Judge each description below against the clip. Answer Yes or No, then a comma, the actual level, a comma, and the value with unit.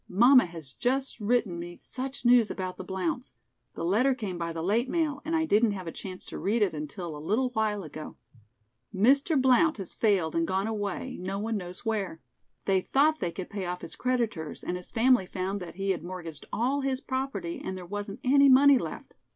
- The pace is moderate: No, fast, 210 wpm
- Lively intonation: Yes, wide, 6.0 semitones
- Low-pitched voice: No, high, 205 Hz